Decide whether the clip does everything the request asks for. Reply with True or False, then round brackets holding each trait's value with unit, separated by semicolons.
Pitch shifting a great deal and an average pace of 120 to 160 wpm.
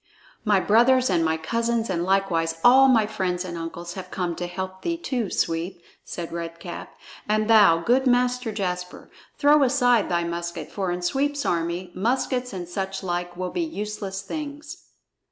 False (5.8 semitones; 170 wpm)